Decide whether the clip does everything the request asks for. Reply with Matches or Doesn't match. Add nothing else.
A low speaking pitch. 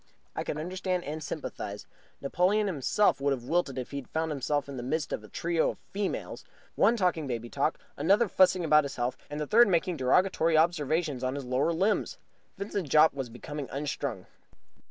Doesn't match